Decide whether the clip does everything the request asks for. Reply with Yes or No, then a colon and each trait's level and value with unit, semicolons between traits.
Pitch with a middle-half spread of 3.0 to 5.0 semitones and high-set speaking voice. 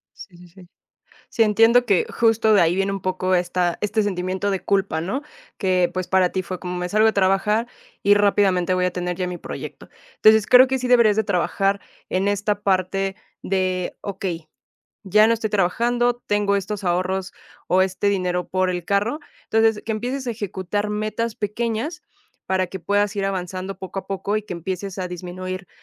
No: narrow, 2.6 semitones; high, 195 Hz